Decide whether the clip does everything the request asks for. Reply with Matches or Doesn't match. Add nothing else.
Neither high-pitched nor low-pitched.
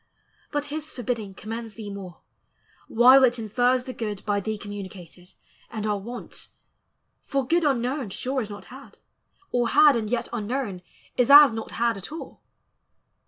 Doesn't match